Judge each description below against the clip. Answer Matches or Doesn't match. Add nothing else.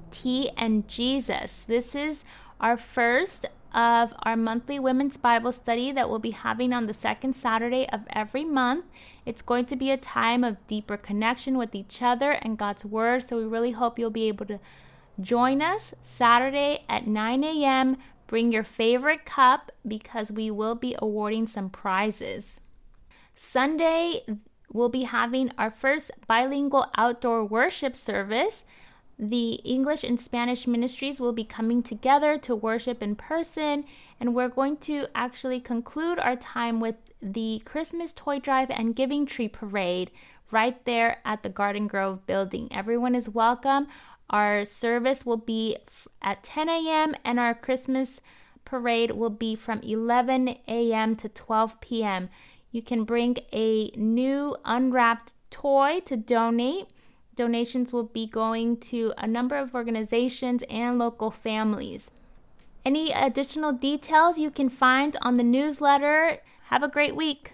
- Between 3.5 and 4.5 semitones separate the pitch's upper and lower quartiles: Doesn't match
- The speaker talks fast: Doesn't match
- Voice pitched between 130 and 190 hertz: Doesn't match